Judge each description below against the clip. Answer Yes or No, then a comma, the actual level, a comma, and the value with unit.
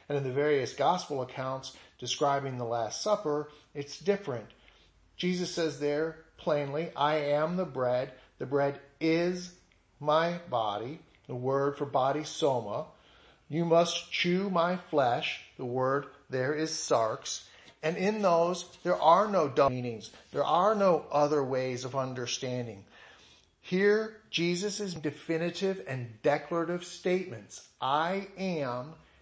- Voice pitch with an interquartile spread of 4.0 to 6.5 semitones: Yes, average, 4.7 semitones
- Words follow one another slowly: Yes, slow, 130 wpm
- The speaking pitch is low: No, medium, 150 Hz